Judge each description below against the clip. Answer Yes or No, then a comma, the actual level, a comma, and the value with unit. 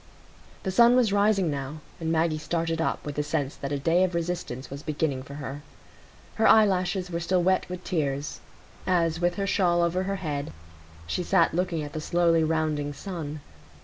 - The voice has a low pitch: No, medium, 165 Hz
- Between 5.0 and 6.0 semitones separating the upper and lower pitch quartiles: No, average, 3.5 semitones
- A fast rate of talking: No, average, 185 wpm